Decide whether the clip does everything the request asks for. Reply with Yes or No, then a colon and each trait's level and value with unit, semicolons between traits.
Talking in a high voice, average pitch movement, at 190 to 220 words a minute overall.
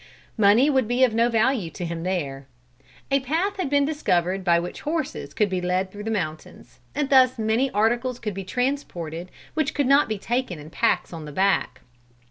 No: high, 220 Hz; wide, 6.8 semitones; average, 195 wpm